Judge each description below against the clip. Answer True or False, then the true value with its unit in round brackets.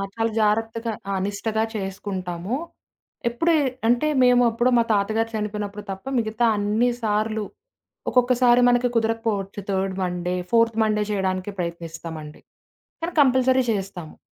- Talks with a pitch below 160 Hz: False (215 Hz)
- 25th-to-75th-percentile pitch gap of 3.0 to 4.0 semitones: True (3.4 semitones)